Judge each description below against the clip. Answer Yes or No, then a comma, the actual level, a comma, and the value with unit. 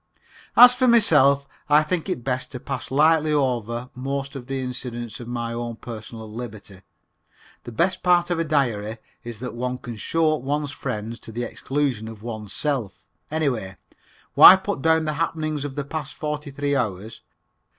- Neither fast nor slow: Yes, average, 170 wpm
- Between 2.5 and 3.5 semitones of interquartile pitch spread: No, average, 4.4 semitones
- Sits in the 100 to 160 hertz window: Yes, low, 135 Hz